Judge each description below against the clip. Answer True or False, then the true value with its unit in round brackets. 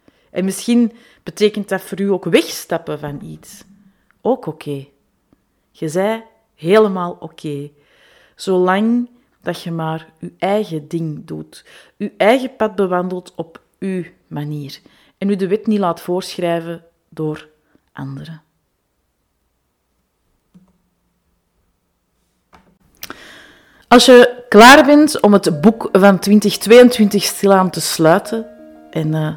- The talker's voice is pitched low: False (185 Hz)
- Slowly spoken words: True (115 wpm)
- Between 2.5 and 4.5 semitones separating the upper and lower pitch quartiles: False (5.1 semitones)